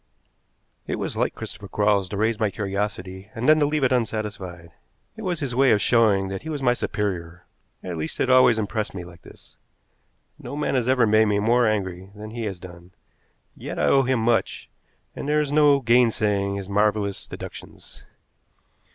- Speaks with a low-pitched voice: Yes, low, 110 Hz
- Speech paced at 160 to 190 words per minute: Yes, average, 185 wpm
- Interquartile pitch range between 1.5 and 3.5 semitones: No, average, 4.3 semitones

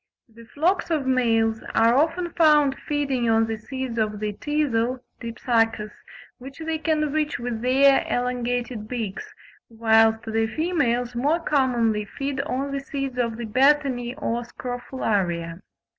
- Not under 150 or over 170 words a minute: No, average, 140 wpm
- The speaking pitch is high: Yes, high, 245 Hz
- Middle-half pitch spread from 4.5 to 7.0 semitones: No, average, 3.8 semitones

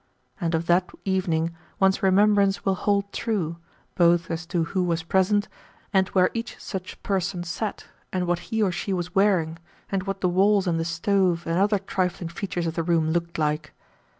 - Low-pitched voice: No, medium, 180 Hz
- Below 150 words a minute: No, average, 185 wpm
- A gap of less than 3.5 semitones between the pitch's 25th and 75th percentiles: Yes, narrow, 2.6 semitones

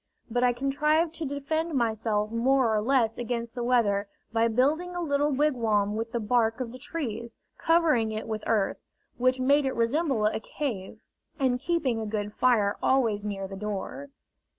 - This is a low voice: No, high, 240 Hz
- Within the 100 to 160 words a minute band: No, average, 175 wpm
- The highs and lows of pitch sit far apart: No, average, 4.1 semitones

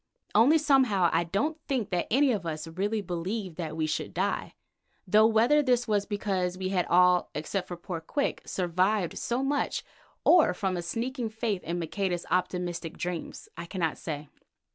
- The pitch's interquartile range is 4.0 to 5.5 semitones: Yes, average, 4.4 semitones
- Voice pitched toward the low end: No, high, 190 Hz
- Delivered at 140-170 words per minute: Yes, average, 165 wpm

